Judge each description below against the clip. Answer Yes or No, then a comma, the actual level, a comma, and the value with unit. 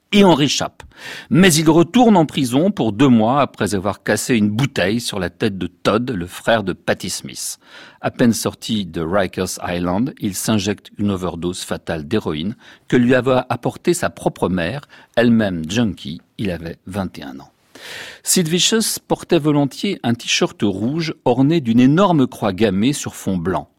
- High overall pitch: No, low, 125 Hz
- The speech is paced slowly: No, average, 165 wpm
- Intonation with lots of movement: Yes, wide, 7.6 semitones